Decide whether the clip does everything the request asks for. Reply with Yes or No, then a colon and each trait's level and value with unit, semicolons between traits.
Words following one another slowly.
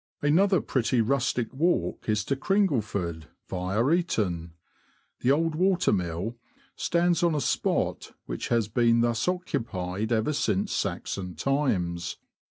Yes: slow, 125 wpm